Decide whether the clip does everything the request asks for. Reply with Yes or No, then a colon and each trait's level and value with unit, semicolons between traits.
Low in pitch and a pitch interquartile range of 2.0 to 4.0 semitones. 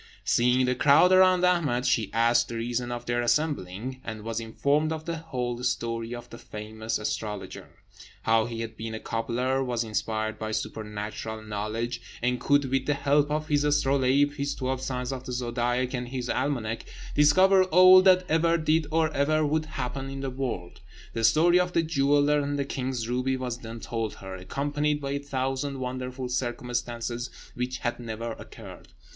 Yes: low, 125 Hz; average, 3.7 semitones